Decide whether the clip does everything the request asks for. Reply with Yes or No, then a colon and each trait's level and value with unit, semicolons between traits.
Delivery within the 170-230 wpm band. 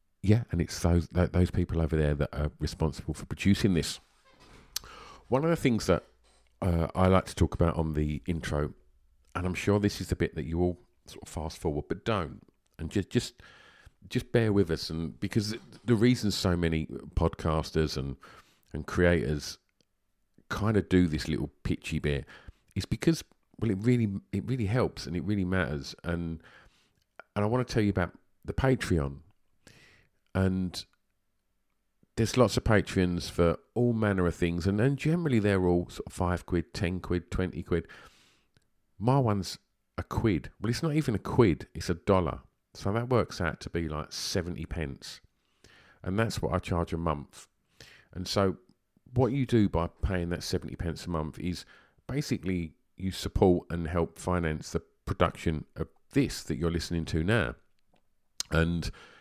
Yes: average, 175 wpm